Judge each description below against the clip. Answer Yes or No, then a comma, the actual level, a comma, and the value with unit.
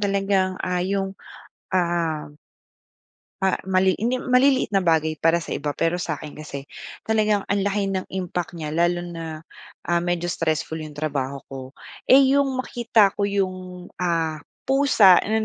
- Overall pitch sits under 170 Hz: No, medium, 180 Hz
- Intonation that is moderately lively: Yes, average, 3.6 semitones